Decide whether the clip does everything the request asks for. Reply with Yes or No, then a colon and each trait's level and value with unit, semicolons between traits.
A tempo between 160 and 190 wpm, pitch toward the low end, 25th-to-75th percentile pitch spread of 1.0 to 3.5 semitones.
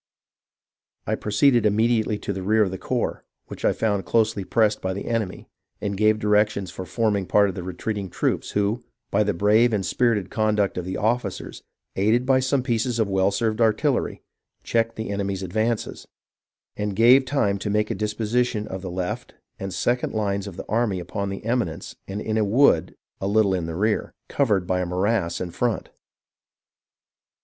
Yes: average, 180 wpm; low, 105 Hz; average, 2.7 semitones